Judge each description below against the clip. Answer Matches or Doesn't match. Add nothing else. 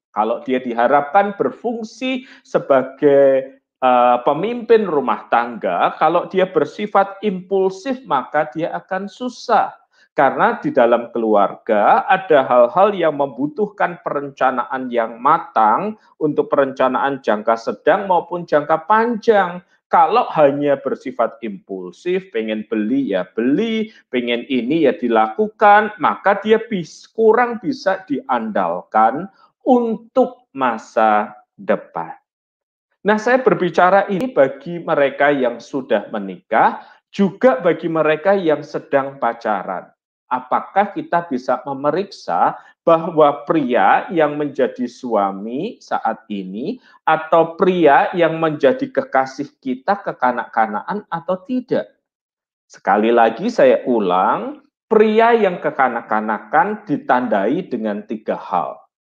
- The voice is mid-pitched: Matches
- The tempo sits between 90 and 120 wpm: Matches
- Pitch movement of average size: Doesn't match